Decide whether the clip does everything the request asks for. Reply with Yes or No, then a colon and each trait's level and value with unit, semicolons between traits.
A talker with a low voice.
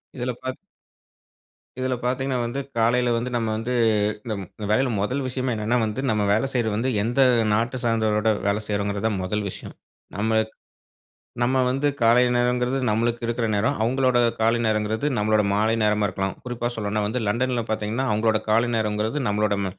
Yes: low, 115 Hz